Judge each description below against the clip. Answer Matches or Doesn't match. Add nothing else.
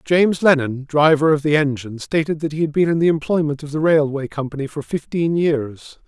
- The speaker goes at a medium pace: Doesn't match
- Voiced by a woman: Doesn't match